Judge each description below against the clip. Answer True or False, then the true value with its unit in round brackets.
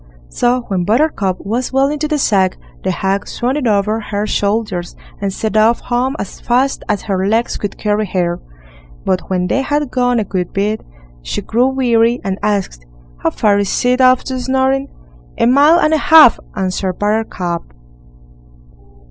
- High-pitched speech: True (220 Hz)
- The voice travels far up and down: False (4.7 semitones)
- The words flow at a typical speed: True (170 wpm)